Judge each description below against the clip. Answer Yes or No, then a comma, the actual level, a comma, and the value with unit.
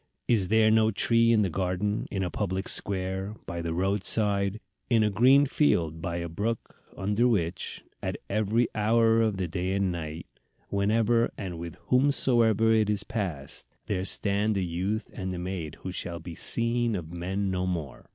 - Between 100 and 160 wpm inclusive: No, average, 175 wpm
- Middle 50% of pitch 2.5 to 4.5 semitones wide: Yes, average, 3.6 semitones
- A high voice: No, low, 100 Hz